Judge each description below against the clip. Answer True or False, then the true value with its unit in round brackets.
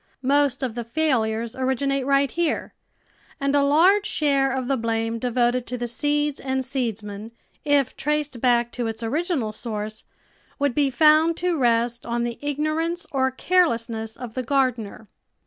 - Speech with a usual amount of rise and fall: True (3.8 semitones)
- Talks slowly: False (160 wpm)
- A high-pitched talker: True (260 Hz)